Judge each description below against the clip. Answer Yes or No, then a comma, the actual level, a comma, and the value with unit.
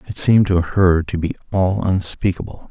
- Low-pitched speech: Yes, very low, 90 Hz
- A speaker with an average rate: Yes, average, 180 wpm